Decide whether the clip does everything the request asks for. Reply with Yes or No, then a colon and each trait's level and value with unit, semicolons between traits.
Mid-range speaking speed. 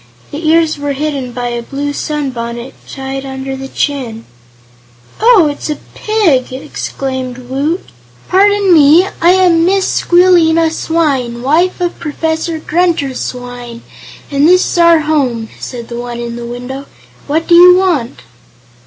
Yes: average, 145 wpm